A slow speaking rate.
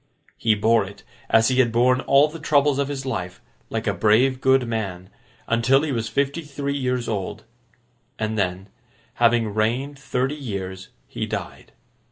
No: average, 165 wpm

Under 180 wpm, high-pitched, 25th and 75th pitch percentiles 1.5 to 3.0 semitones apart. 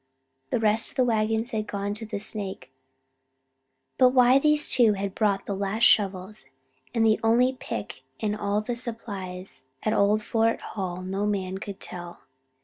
Yes: average, 170 wpm; high, 210 Hz; average, 2.7 semitones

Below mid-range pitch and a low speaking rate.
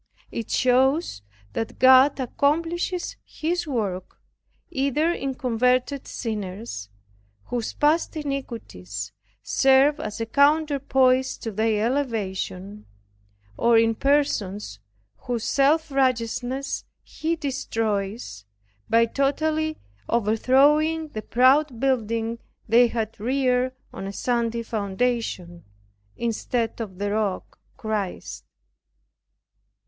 No: high, 245 Hz; slow, 95 wpm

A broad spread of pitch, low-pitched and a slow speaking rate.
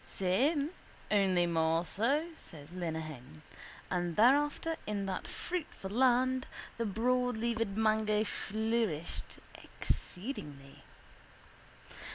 No: wide, 6.1 semitones; high, 215 Hz; slow, 85 wpm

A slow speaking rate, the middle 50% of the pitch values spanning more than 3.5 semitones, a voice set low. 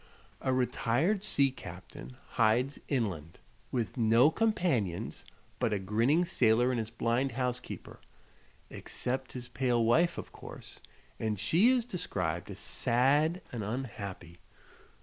Yes: slow, 125 wpm; average, 4.2 semitones; low, 120 Hz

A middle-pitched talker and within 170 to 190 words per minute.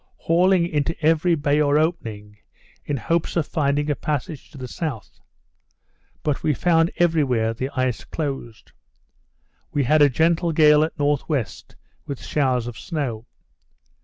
No: medium, 145 Hz; average, 145 wpm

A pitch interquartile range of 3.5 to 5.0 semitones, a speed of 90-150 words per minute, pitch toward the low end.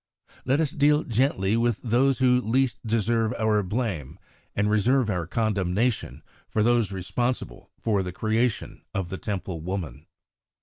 Yes: average, 4.2 semitones; average, 140 wpm; low, 110 Hz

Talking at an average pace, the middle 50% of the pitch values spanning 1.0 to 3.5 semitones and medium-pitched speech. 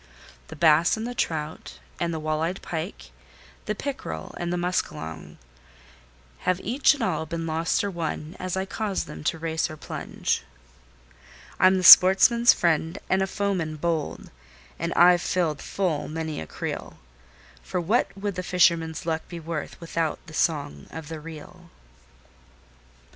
Yes: average, 155 wpm; average, 2.8 semitones; medium, 170 Hz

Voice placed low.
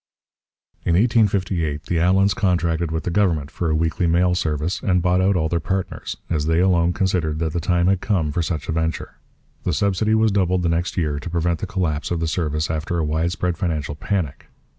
Yes: very low, 85 Hz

